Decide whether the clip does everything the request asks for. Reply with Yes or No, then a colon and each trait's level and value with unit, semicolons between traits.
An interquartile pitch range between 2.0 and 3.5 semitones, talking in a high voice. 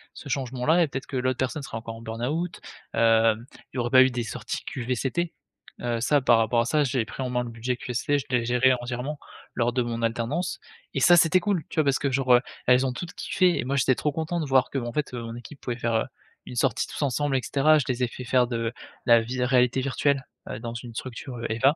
No: average, 2.9 semitones; low, 125 Hz